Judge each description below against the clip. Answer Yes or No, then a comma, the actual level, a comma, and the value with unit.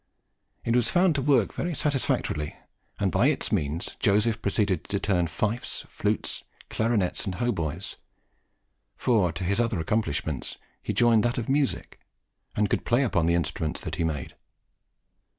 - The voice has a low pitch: Yes, low, 105 Hz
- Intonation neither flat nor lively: No, wide, 5.9 semitones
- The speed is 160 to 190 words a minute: No, average, 150 wpm